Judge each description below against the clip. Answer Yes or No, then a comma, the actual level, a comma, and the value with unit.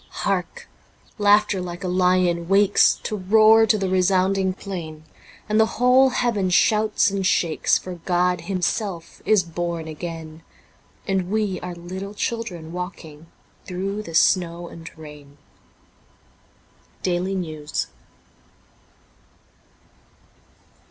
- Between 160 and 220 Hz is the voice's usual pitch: Yes, medium, 185 Hz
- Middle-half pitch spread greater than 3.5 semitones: No, average, 3.0 semitones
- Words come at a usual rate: No, slow, 110 wpm